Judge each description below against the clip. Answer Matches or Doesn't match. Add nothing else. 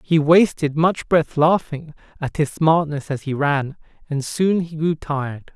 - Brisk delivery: Doesn't match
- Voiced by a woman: Doesn't match